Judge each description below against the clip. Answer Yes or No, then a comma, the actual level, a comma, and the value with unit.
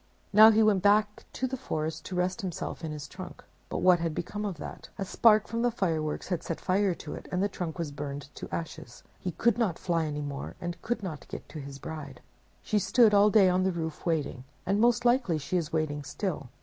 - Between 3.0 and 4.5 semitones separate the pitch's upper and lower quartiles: No, average, 5.1 semitones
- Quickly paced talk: Yes, fast, 230 wpm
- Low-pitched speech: No, medium, 180 Hz